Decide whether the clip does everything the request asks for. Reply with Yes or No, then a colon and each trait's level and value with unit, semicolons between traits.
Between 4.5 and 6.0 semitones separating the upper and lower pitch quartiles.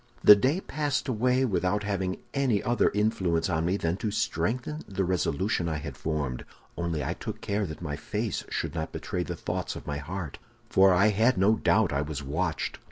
Yes: average, 5.1 semitones